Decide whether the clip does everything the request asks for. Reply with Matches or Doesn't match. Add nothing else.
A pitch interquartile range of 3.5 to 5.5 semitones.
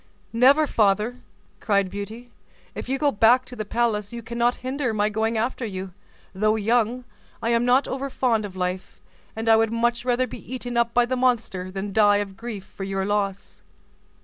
Doesn't match